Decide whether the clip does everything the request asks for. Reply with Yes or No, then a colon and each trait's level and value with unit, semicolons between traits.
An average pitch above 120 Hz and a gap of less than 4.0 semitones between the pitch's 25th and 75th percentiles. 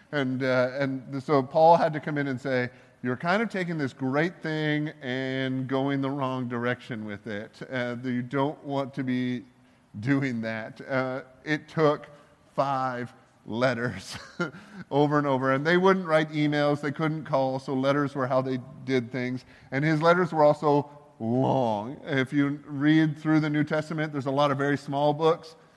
Yes: medium, 140 Hz; average, 2.7 semitones